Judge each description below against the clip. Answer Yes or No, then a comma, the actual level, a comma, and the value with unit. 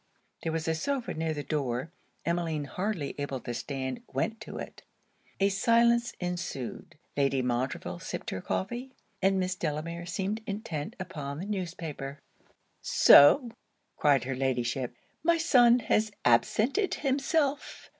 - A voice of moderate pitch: Yes, medium, 170 Hz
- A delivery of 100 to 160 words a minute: Yes, slow, 135 wpm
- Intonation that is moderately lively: No, wide, 7.9 semitones